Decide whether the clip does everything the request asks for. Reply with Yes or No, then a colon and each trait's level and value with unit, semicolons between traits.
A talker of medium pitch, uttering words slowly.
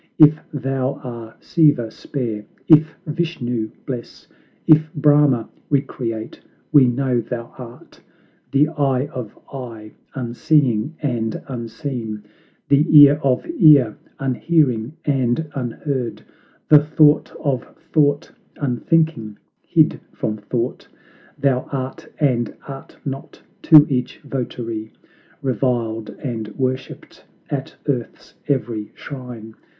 No: low, 130 Hz; slow, 105 wpm